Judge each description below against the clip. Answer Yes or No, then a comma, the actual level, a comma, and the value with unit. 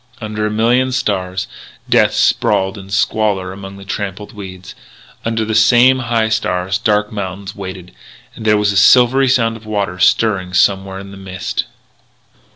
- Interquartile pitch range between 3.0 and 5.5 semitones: No, narrow, 2.5 semitones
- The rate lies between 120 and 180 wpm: Yes, average, 160 wpm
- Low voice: Yes, low, 105 Hz